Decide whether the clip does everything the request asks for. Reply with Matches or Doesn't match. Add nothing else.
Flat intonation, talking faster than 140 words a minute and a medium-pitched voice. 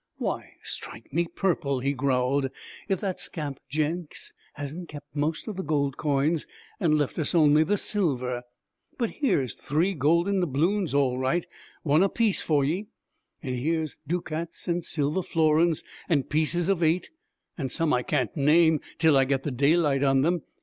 Doesn't match